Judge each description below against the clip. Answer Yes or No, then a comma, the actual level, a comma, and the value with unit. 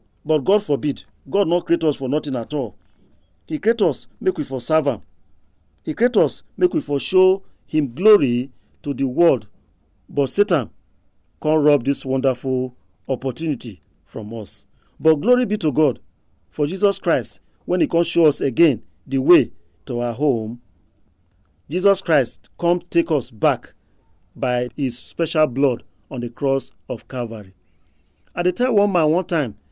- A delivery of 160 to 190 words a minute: Yes, average, 165 wpm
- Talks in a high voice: No, low, 135 Hz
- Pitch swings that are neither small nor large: No, wide, 8.0 semitones